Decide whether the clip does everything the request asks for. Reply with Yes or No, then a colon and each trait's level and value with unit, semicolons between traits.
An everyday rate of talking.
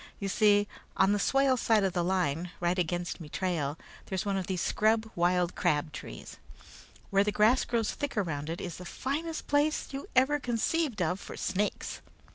Yes: average, 180 wpm